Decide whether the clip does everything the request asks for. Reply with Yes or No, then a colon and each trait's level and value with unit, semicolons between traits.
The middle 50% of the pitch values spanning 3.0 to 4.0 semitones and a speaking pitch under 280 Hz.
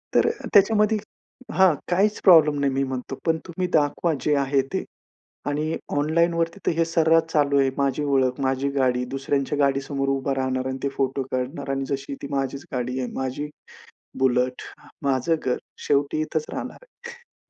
Yes: average, 3.4 semitones; medium, 140 Hz